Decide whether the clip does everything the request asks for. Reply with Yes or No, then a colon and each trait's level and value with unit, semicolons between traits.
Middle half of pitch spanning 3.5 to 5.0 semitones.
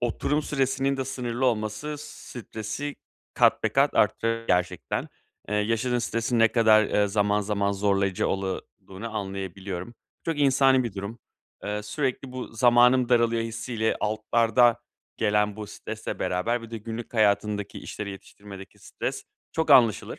No: average, 3.1 semitones